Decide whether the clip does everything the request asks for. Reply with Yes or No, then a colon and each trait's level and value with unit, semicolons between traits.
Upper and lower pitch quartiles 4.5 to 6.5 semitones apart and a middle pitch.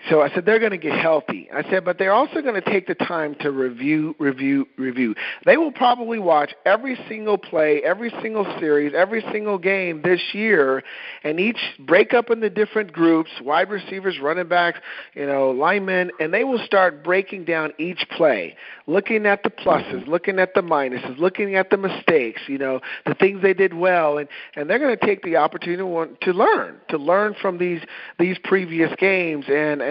Yes: average, 5.0 semitones; medium, 180 Hz